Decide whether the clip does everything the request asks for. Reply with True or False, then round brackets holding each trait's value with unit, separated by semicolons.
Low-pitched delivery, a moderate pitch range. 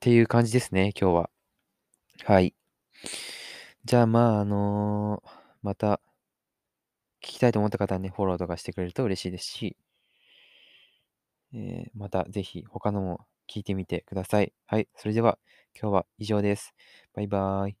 True (105 Hz; 3.5 semitones)